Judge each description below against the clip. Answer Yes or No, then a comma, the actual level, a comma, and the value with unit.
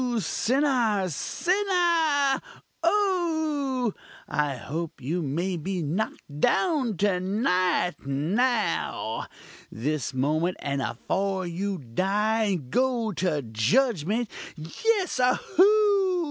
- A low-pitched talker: No, high, 200 Hz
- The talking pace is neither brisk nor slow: No, slow, 90 wpm